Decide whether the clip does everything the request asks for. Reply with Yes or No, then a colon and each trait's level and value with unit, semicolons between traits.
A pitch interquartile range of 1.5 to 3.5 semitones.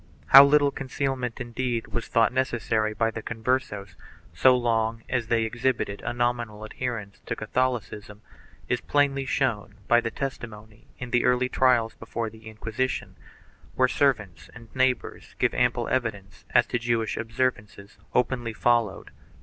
Yes: narrow, 2.6 semitones